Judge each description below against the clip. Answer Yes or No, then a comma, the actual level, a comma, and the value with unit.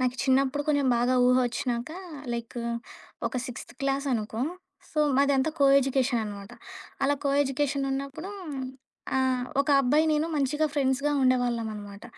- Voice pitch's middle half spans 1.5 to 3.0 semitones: Yes, narrow, 2.4 semitones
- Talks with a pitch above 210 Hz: Yes, very high, 265 Hz